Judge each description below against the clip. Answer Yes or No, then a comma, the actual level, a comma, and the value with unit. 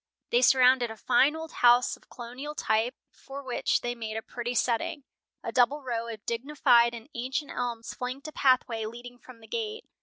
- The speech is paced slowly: No, average, 185 wpm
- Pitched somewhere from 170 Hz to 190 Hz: No, high, 245 Hz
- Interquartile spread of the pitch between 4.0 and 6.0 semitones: No, narrow, 2.5 semitones